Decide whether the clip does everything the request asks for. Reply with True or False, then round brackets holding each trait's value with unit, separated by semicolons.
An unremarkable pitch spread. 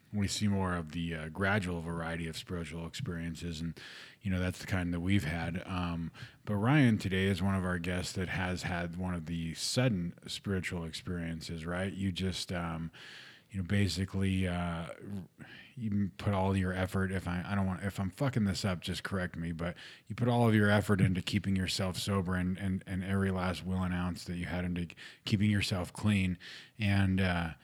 False (2.2 semitones)